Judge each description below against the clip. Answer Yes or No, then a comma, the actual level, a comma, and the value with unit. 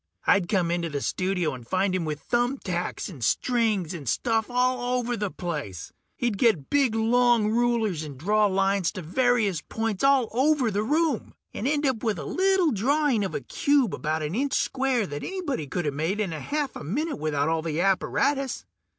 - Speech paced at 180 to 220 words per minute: Yes, average, 195 wpm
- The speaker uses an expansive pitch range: Yes, wide, 6.8 semitones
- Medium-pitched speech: No, high, 215 Hz